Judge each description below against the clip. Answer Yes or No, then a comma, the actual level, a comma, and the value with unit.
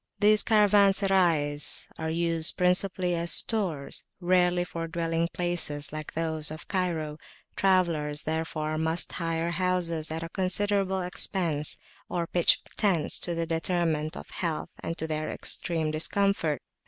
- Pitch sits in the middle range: Yes, medium, 170 Hz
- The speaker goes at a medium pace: No, slow, 130 wpm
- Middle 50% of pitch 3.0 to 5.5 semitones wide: No, narrow, 2.5 semitones